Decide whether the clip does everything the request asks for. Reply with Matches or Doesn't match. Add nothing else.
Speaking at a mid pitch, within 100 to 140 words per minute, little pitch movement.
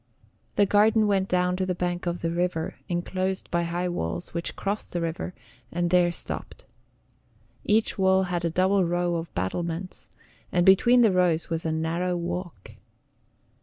Doesn't match